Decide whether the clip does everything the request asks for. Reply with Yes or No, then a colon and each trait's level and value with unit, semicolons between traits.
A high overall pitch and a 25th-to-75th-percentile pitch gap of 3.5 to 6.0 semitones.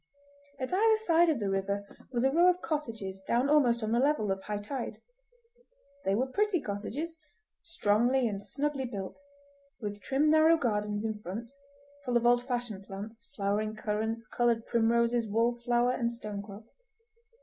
Yes: high, 235 Hz; average, 4.3 semitones